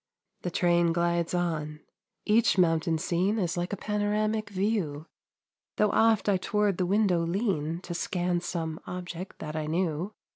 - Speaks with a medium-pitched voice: Yes, medium, 175 Hz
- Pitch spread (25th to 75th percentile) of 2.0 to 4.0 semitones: Yes, average, 3.5 semitones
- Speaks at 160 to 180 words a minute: No, average, 150 wpm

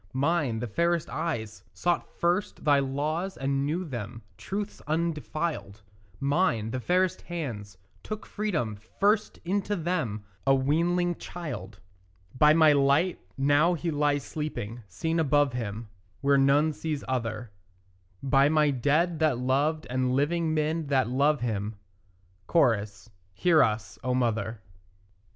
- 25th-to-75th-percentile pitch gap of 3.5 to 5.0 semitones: No, wide, 5.4 semitones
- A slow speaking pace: Yes, slow, 130 wpm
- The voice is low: No, medium, 145 Hz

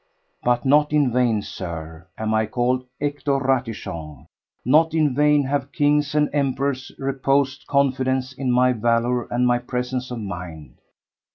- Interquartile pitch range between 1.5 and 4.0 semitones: Yes, average, 3.1 semitones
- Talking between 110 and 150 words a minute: Yes, average, 145 wpm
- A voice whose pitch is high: No, low, 130 Hz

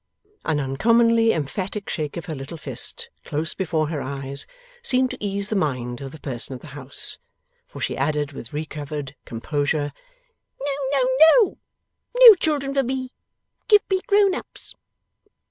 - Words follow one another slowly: No, average, 155 wpm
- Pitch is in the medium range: Yes, medium, 155 Hz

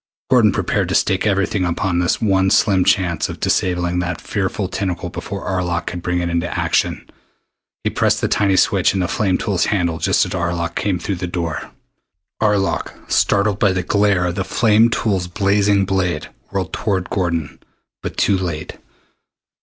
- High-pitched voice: No, very low, 95 Hz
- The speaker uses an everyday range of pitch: No, narrow, 2.3 semitones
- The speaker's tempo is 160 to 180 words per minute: Yes, average, 170 wpm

